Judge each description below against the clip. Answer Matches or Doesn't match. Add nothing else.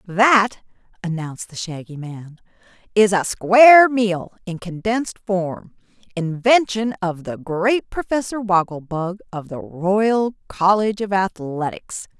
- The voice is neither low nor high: Doesn't match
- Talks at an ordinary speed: Doesn't match